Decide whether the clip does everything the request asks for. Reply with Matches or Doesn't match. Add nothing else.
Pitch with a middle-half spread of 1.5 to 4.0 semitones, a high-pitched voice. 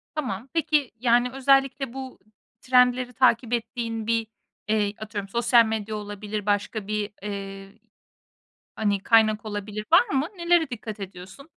Matches